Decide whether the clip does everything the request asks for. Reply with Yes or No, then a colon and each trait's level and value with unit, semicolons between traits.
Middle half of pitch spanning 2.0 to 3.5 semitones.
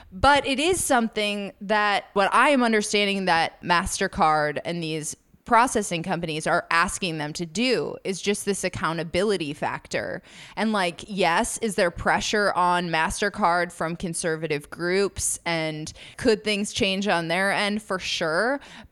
No: average, 3.9 semitones